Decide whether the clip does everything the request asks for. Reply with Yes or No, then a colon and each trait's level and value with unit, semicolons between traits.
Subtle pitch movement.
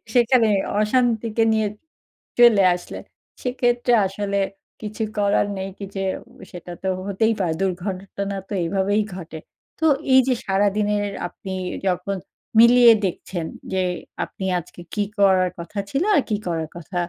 No: average, 3.1 semitones